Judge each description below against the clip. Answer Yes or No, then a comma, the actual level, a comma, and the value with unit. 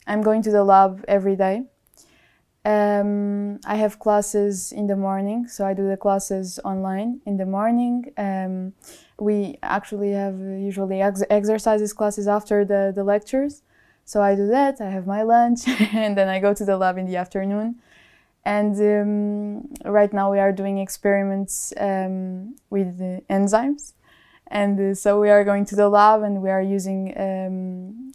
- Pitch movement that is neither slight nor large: No, narrow, 1.3 semitones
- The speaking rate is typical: Yes, average, 170 wpm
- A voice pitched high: Yes, high, 205 Hz